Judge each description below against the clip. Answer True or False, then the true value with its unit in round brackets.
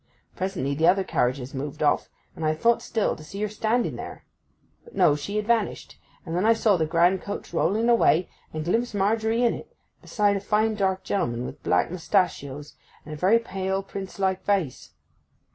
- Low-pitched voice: False (190 Hz)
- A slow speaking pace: False (190 wpm)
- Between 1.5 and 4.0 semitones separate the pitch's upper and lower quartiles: False (5.3 semitones)